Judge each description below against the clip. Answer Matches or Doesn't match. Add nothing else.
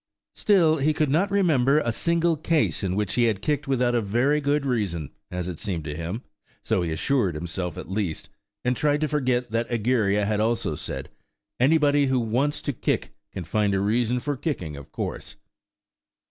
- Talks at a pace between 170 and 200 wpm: Matches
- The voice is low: Matches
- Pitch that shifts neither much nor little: Doesn't match